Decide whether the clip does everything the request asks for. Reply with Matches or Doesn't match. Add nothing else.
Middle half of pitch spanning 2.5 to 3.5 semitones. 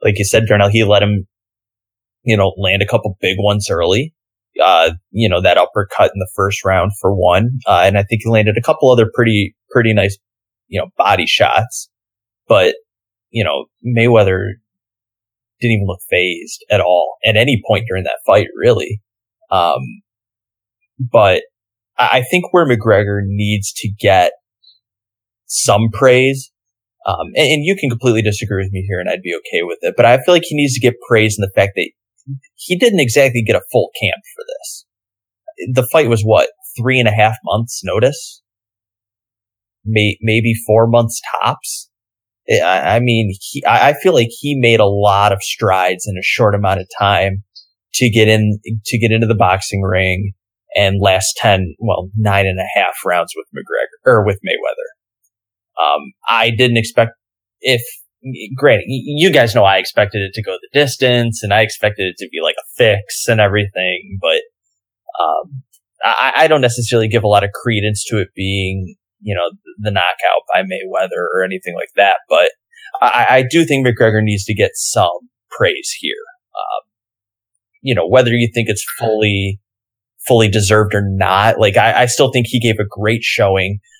Matches